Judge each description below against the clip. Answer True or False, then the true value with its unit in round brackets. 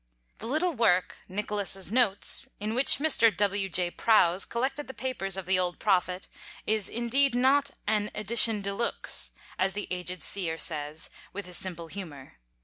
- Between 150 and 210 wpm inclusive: True (160 wpm)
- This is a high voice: True (200 Hz)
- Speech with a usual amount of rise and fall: True (4.5 semitones)